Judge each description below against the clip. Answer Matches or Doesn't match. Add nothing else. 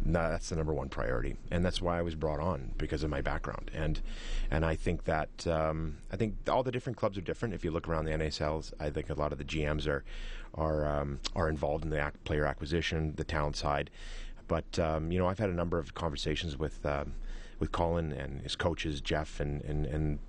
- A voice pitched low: Matches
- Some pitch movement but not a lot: Doesn't match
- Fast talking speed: Matches